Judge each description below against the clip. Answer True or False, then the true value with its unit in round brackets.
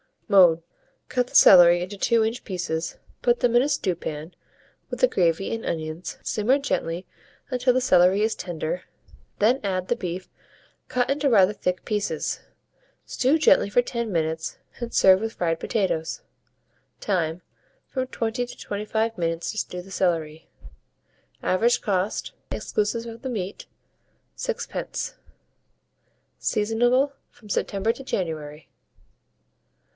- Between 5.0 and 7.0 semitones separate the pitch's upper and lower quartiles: True (5.3 semitones)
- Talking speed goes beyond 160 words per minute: False (135 wpm)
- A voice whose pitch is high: True (200 Hz)